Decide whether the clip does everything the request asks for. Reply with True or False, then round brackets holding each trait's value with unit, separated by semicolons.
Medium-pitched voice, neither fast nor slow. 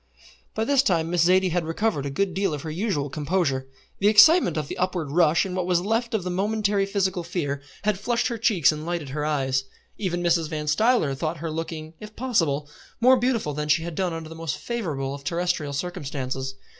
False (170 Hz; 210 wpm)